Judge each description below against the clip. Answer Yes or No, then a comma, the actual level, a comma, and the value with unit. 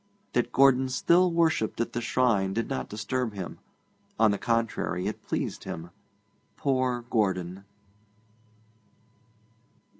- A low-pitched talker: Yes, low, 115 Hz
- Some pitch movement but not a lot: Yes, average, 4.1 semitones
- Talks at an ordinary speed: No, slow, 115 wpm